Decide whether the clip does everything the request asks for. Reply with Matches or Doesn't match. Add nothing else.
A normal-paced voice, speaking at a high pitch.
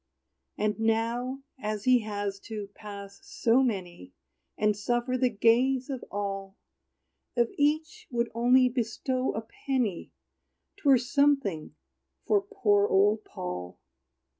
Doesn't match